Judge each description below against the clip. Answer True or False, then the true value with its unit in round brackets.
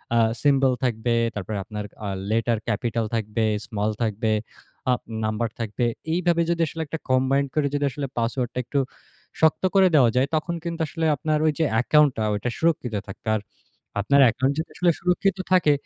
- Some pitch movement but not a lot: False (5.7 semitones)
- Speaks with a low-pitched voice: True (130 Hz)